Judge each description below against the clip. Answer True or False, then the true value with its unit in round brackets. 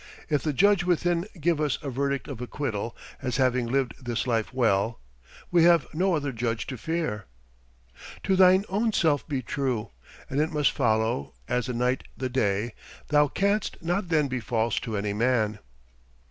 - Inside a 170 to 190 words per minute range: True (175 wpm)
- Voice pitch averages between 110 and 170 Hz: True (135 Hz)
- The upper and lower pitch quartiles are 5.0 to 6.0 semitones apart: True (5.6 semitones)